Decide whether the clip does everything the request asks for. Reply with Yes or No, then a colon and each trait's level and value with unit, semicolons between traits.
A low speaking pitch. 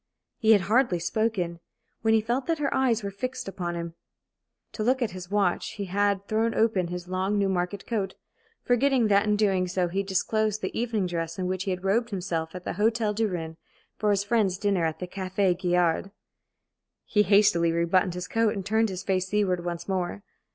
No: high, 195 Hz